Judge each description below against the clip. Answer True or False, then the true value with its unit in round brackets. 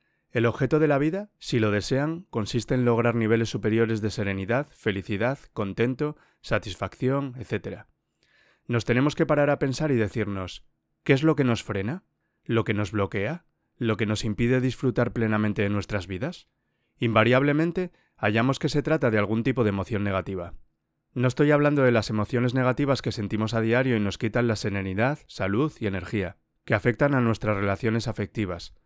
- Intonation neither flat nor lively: True (4.1 semitones)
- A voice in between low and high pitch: False (115 Hz)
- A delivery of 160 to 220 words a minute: True (170 wpm)